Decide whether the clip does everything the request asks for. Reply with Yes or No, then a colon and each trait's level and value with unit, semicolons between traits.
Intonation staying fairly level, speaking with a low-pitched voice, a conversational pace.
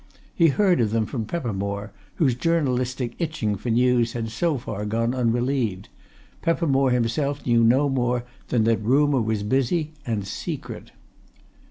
No: average, 3.6 semitones; low, 125 Hz; average, 145 wpm